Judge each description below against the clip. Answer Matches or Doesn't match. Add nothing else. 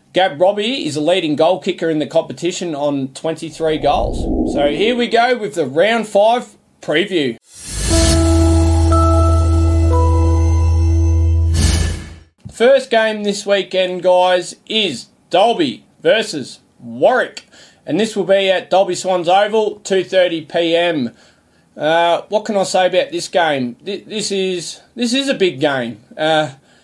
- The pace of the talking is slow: Matches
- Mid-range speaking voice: Matches